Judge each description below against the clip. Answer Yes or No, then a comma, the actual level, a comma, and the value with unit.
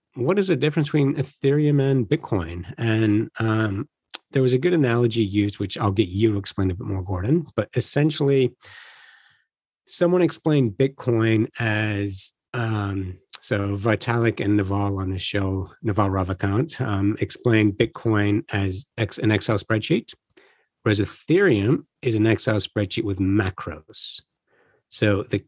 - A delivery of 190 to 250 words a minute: No, average, 140 wpm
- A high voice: No, low, 110 Hz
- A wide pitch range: No, average, 4.3 semitones